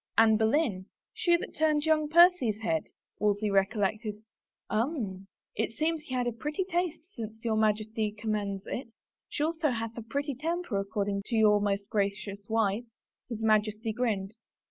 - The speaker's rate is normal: Yes, average, 165 wpm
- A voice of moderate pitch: No, high, 220 Hz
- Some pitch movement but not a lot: No, wide, 6.0 semitones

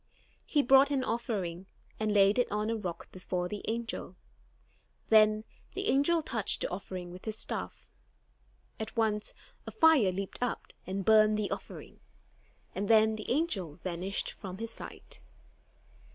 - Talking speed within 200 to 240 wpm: No, average, 150 wpm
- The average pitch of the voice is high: Yes, high, 215 Hz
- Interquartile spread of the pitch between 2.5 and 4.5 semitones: Yes, average, 3.6 semitones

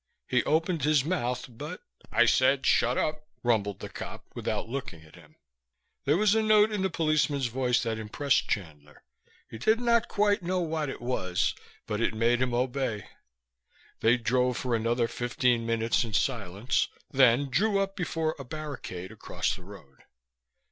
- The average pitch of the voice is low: Yes, low, 125 Hz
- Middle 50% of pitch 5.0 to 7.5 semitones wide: Yes, wide, 5.5 semitones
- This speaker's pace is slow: No, average, 165 wpm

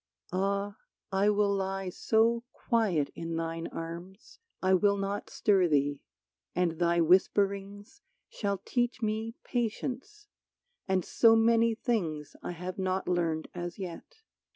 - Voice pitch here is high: Yes, high, 195 Hz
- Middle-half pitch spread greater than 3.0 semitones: Yes, average, 4.0 semitones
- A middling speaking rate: No, slow, 130 wpm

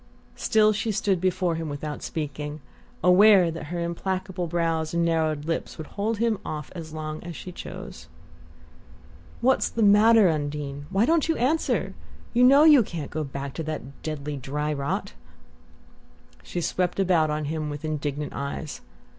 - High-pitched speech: No, medium, 165 Hz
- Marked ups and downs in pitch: No, average, 4.6 semitones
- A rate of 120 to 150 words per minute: No, average, 160 wpm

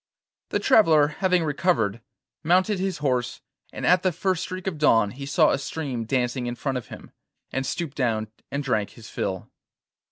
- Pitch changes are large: Yes, wide, 6.4 semitones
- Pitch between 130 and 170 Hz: Yes, medium, 140 Hz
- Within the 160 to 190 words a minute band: Yes, average, 180 wpm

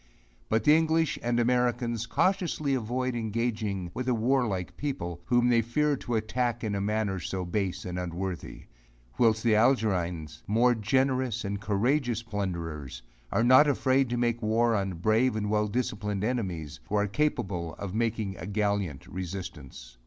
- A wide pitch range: No, average, 4.1 semitones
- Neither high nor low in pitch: No, low, 110 Hz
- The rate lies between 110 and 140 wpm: No, average, 155 wpm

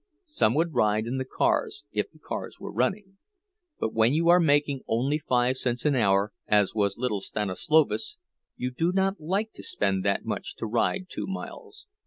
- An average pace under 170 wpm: No, average, 185 wpm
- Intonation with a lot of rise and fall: Yes, wide, 7.8 semitones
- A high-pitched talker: No, low, 130 Hz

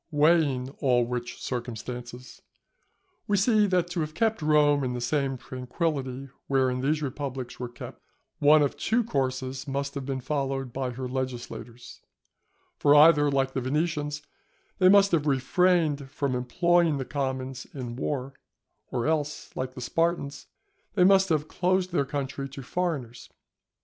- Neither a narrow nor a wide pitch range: Yes, average, 3.5 semitones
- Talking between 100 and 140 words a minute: No, average, 150 wpm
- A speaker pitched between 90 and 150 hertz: Yes, medium, 140 Hz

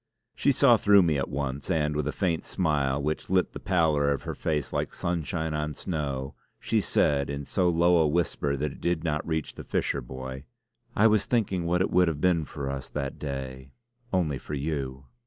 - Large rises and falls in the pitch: No, average, 3.9 semitones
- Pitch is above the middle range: No, very low, 75 Hz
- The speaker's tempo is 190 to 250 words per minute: Yes, fast, 205 wpm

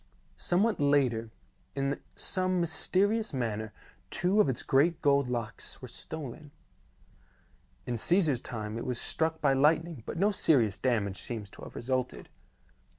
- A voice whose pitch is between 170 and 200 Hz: No, medium, 140 Hz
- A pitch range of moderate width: No, wide, 5.8 semitones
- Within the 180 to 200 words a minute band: No, average, 140 wpm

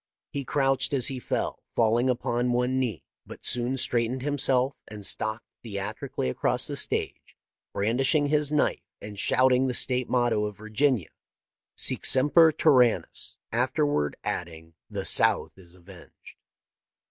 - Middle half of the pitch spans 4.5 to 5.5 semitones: No, average, 4.0 semitones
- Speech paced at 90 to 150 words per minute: Yes, average, 145 wpm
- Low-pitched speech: Yes, low, 125 Hz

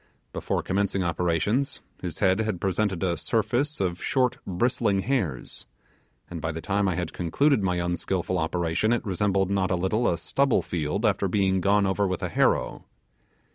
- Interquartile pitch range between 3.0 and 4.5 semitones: Yes, average, 3.4 semitones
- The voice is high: No, very low, 95 Hz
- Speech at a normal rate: Yes, average, 170 wpm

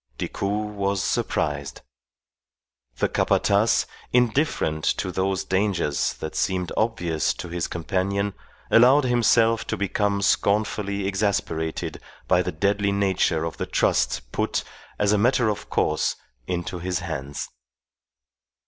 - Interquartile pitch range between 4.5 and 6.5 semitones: No, average, 3.4 semitones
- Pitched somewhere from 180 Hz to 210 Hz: No, low, 100 Hz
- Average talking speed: No, slow, 120 wpm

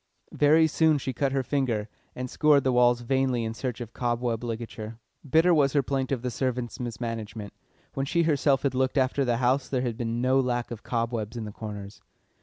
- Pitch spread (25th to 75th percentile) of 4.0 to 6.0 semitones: No, narrow, 2.6 semitones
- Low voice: Yes, low, 125 Hz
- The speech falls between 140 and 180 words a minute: No, fast, 205 wpm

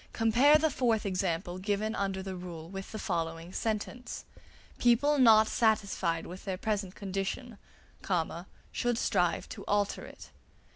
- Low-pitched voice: No, high, 200 Hz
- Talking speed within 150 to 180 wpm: No, slow, 135 wpm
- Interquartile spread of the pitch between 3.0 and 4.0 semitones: Yes, average, 3.5 semitones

